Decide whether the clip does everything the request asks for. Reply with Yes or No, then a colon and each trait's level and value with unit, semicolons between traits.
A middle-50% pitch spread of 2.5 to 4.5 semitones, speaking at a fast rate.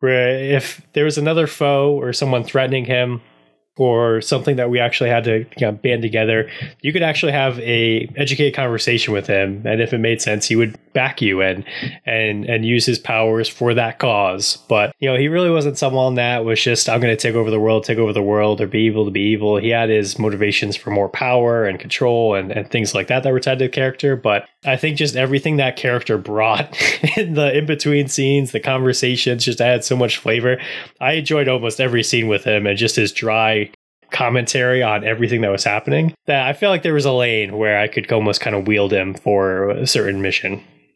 Yes: average, 3.6 semitones; fast, 215 wpm